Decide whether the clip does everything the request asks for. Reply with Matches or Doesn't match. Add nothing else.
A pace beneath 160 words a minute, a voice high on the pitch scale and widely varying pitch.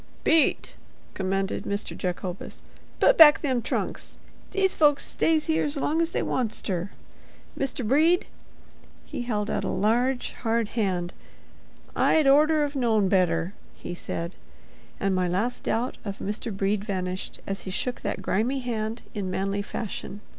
Matches